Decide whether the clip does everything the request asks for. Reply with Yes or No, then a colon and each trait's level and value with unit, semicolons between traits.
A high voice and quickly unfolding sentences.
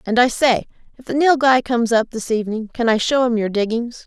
Yes: high, 240 Hz; fast, 235 wpm